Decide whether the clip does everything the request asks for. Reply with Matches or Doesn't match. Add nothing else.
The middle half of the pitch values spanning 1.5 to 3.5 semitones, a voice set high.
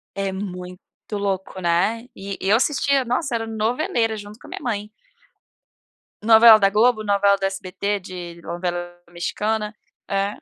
Matches